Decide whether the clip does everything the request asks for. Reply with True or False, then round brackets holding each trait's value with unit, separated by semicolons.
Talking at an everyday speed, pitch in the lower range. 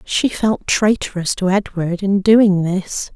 False (150 wpm; 195 Hz)